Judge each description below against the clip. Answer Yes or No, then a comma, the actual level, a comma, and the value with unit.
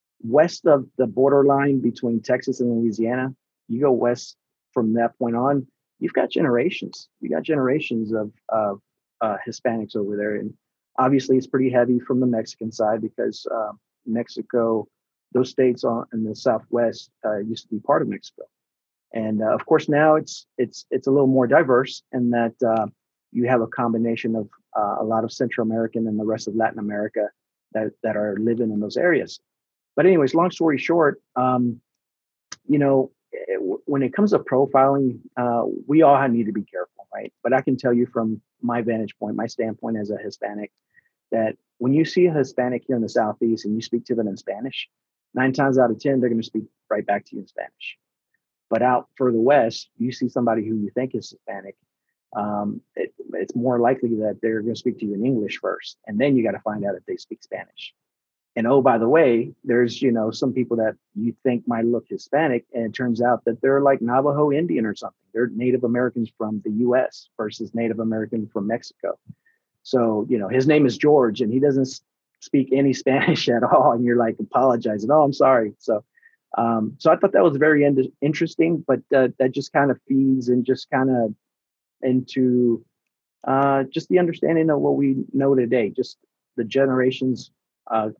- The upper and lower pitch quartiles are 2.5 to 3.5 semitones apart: Yes, average, 3.1 semitones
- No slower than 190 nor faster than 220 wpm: Yes, average, 200 wpm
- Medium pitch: No, low, 125 Hz